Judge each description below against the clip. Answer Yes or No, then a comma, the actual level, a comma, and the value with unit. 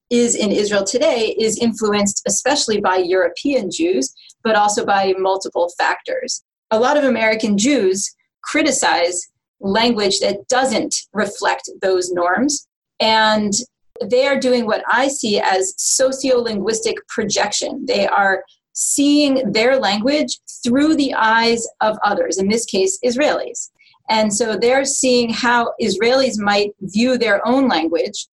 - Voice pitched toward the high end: Yes, high, 230 Hz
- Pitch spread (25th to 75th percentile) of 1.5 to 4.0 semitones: No, average, 4.7 semitones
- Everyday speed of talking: No, slow, 130 wpm